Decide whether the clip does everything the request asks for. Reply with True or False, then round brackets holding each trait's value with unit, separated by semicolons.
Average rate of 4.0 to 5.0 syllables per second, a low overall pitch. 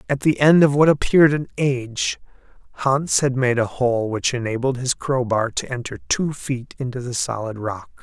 True (4.9 syllables/s; 125 Hz)